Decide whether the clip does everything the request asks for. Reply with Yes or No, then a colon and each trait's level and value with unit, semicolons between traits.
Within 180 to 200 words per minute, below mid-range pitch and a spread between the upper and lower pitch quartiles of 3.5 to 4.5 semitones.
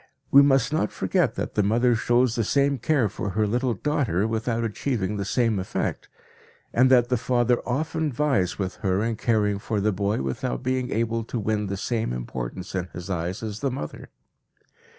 Yes: average, 190 wpm; low, 115 Hz; average, 4.1 semitones